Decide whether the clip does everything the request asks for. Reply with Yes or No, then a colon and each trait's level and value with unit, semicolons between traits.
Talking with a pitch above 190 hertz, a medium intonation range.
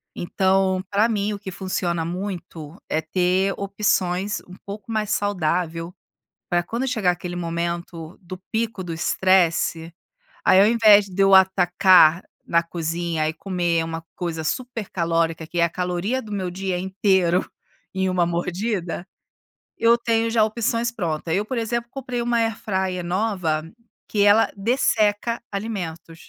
No: medium, 185 Hz; average, 3.5 semitones